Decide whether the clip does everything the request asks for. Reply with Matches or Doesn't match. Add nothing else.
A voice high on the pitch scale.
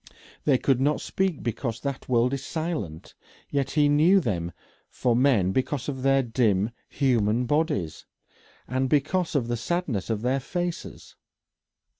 Doesn't match